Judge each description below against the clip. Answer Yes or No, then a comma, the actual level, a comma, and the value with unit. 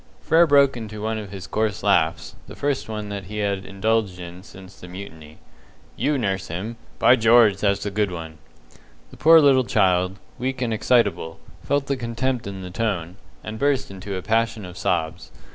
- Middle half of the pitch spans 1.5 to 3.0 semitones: No, average, 4.1 semitones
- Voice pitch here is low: Yes, low, 105 Hz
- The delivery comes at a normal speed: Yes, average, 185 wpm